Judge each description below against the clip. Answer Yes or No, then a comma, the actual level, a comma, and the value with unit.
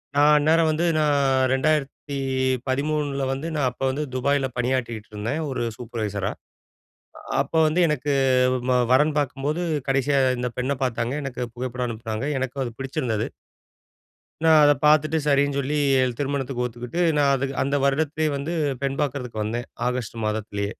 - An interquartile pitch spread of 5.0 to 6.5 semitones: No, average, 3.0 semitones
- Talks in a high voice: No, low, 135 Hz